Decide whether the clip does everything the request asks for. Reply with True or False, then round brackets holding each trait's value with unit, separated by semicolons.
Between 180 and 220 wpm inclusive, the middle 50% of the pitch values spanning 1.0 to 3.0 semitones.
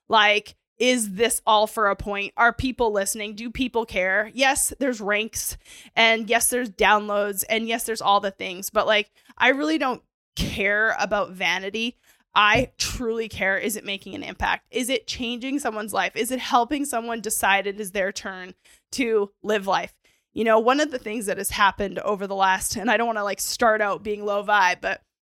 True (195 wpm; 2.7 semitones)